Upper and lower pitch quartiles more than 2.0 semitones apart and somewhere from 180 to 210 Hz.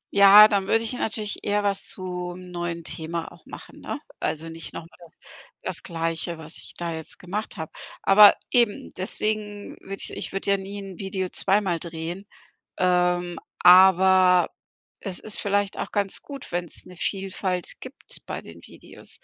Yes: average, 2.7 semitones; medium, 185 Hz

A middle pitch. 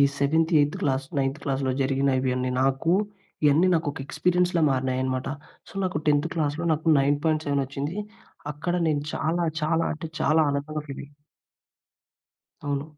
Yes: medium, 145 Hz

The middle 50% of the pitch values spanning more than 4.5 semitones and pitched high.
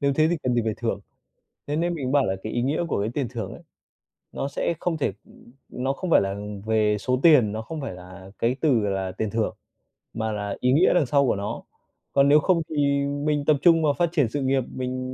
No: average, 5.2 semitones; low, 135 Hz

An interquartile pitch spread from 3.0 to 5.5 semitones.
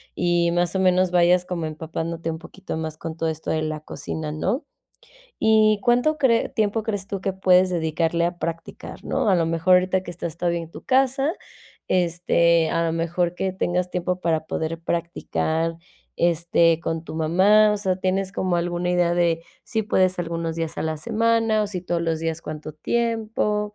No: narrow, 2.6 semitones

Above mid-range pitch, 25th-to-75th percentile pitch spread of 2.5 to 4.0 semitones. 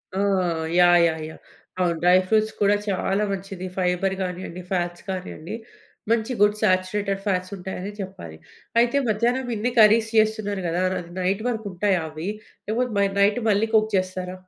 Yes: high, 195 Hz; average, 2.9 semitones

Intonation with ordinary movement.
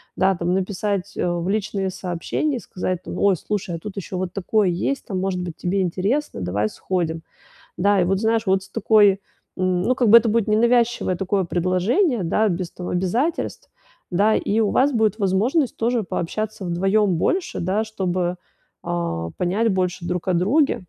Yes: average, 3.4 semitones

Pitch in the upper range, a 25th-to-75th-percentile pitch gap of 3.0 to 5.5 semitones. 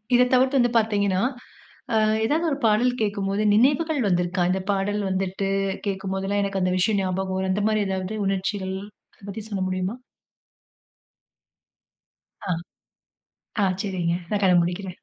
No: high, 195 Hz; narrow, 2.4 semitones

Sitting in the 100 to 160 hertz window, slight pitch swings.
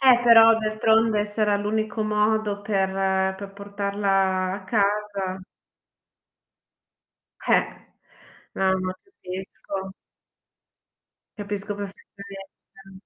No: high, 200 Hz; narrow, 1.8 semitones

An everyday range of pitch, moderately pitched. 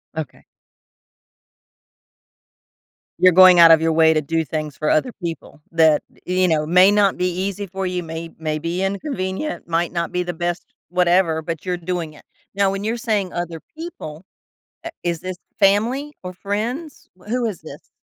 Yes: average, 3.2 semitones; medium, 180 Hz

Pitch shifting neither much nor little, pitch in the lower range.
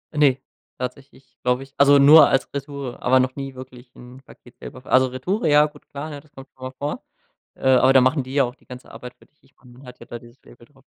No: narrow, 1.9 semitones; low, 130 Hz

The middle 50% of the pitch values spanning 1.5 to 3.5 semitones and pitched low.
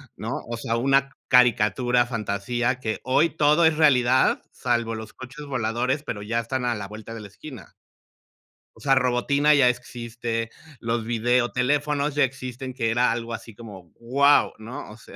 Yes: average, 2.7 semitones; low, 125 Hz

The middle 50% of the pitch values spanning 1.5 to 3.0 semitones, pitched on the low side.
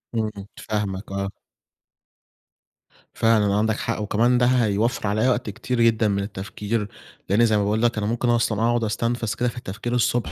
Yes: narrow, 2.4 semitones; low, 110 Hz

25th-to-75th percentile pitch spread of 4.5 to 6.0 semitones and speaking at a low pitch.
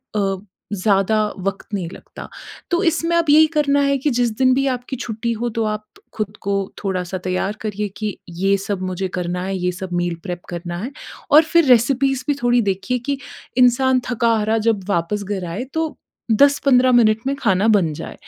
No: average, 5.0 semitones; high, 215 Hz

